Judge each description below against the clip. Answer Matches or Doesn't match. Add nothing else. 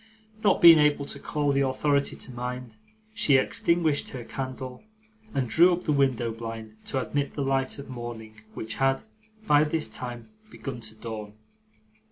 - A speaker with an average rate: Matches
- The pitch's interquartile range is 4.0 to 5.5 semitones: Doesn't match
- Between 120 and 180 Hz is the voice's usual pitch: Matches